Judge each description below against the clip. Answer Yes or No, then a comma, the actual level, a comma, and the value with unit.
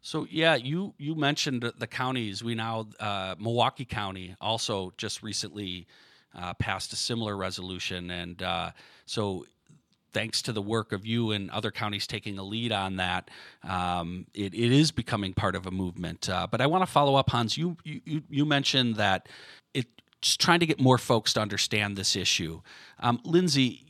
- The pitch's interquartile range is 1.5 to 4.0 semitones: No, average, 5.2 semitones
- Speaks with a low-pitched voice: Yes, low, 110 Hz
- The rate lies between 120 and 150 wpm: No, average, 180 wpm